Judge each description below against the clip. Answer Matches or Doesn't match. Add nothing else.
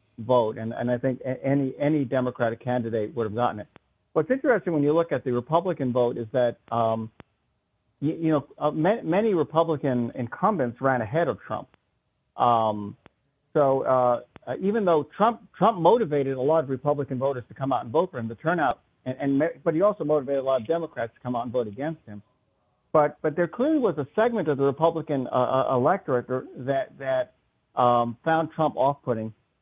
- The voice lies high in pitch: Doesn't match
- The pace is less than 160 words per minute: Doesn't match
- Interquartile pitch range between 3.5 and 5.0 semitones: Matches